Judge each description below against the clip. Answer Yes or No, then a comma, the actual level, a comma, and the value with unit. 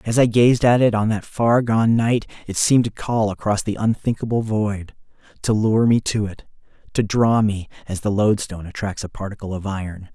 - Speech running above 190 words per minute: Yes, average, 200 wpm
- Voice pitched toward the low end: Yes, low, 105 Hz